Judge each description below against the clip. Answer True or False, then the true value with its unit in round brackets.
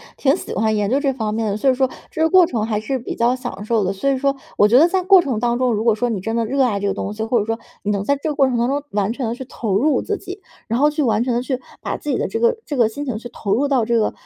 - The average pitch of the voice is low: False (240 Hz)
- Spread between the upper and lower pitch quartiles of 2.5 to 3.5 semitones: False (4.1 semitones)